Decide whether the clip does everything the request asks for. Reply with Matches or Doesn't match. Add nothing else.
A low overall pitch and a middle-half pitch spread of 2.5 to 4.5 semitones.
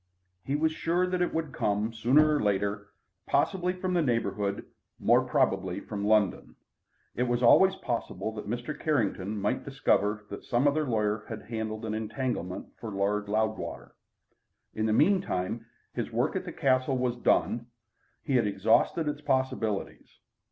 Doesn't match